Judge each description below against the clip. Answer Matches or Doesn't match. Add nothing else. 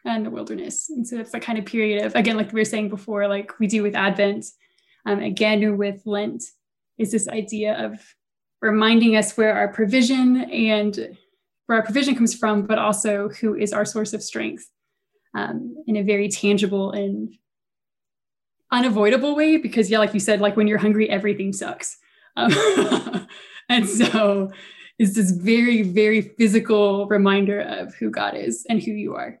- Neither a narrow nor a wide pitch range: Doesn't match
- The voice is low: Doesn't match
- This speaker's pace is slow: Doesn't match